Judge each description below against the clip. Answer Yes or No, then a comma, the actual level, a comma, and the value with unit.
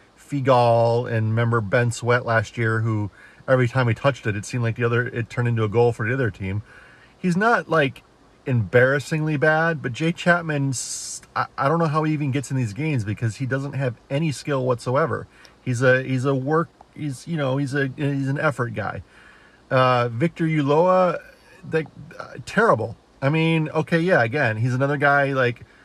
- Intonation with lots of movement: No, average, 4.2 semitones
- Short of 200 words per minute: Yes, average, 190 wpm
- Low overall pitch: Yes, low, 130 Hz